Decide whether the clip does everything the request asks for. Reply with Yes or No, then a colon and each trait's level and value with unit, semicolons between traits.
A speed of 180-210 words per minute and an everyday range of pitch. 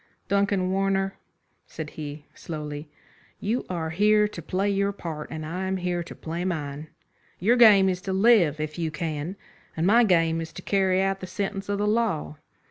Yes: average, 185 wpm; average, 3.7 semitones